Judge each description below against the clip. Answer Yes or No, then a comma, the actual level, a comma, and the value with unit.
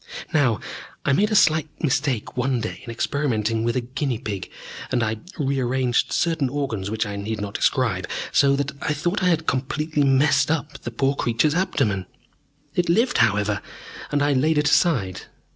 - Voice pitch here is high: No, low, 135 Hz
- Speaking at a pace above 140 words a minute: Yes, average, 175 wpm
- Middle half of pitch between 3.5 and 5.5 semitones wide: Yes, average, 4.8 semitones